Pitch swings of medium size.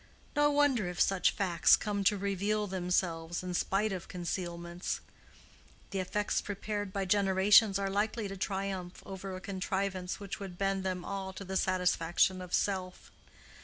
No: narrow, 1.7 semitones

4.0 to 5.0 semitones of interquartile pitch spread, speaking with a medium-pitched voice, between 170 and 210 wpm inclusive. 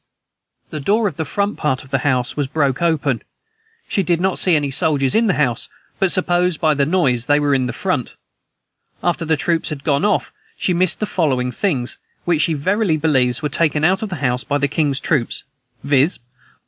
Yes: average, 4.3 semitones; medium, 150 Hz; fast, 205 wpm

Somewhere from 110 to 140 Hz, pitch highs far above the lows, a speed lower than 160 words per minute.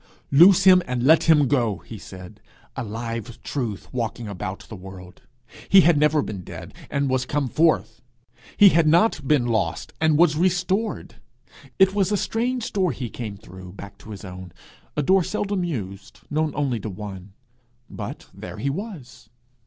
No: low, 135 Hz; wide, 8.7 semitones; average, 170 wpm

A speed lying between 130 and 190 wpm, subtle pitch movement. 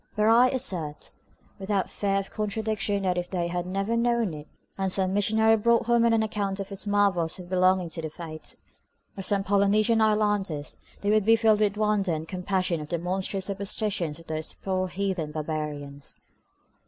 No: average, 180 wpm; average, 3.3 semitones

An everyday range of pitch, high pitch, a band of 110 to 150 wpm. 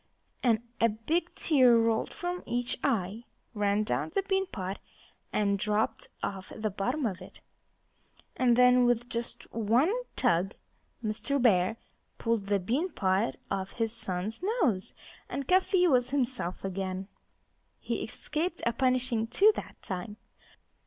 Yes: average, 4.6 semitones; high, 230 Hz; average, 140 wpm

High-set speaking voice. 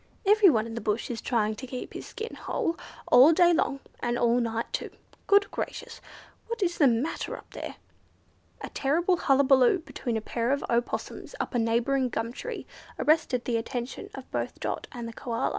Yes: very high, 255 Hz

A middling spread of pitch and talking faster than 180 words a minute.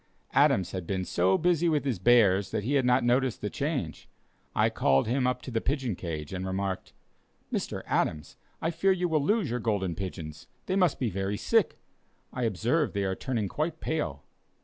No: wide, 7.1 semitones; average, 195 wpm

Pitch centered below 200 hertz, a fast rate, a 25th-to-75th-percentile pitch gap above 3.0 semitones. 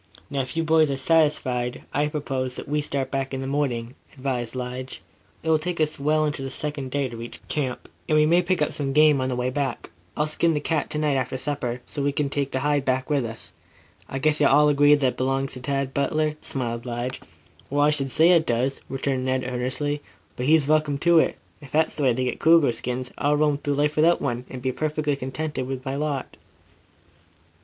No: medium, 140 Hz; fast, 230 wpm; narrow, 2.6 semitones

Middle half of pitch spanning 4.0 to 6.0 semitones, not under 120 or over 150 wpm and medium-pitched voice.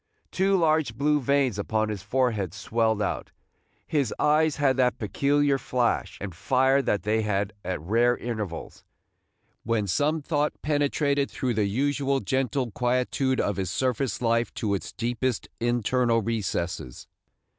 No: average, 4.6 semitones; average, 140 wpm; low, 120 Hz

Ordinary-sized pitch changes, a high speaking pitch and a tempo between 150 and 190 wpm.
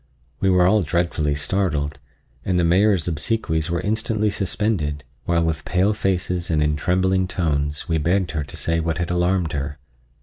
No: average, 3.5 semitones; very low, 85 Hz; average, 170 wpm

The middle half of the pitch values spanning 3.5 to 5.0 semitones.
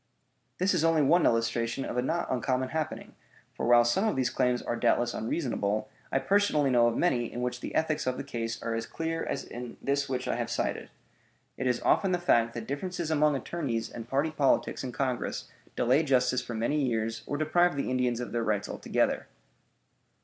Yes: average, 4.4 semitones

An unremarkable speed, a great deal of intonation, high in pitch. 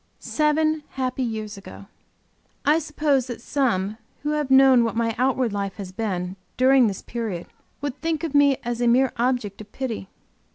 No: average, 170 wpm; average, 4.4 semitones; very high, 250 Hz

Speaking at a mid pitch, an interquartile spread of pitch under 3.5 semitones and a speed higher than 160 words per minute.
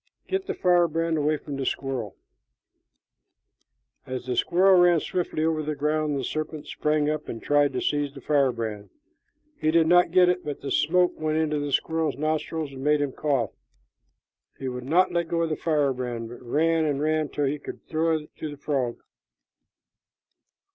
Yes: medium, 150 Hz; average, 2.7 semitones; average, 180 wpm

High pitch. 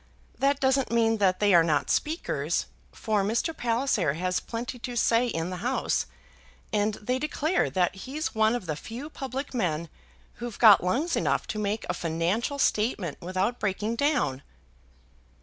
Yes: high, 225 Hz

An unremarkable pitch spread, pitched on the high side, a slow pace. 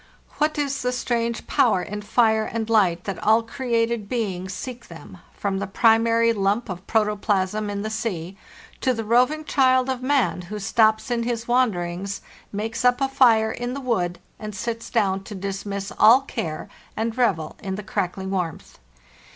No: average, 3.5 semitones; high, 220 Hz; average, 175 wpm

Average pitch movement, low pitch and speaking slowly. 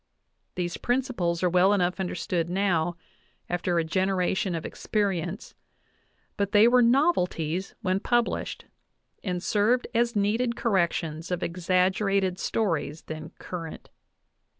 No: average, 3.4 semitones; medium, 185 Hz; slow, 115 wpm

